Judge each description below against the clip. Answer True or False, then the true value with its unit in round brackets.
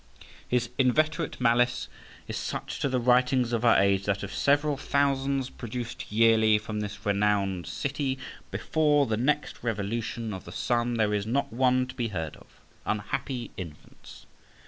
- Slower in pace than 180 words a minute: True (155 wpm)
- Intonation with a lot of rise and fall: False (4.2 semitones)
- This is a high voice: False (120 Hz)